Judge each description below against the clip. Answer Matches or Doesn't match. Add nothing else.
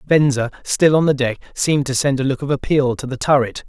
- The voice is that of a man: Matches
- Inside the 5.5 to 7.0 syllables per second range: Matches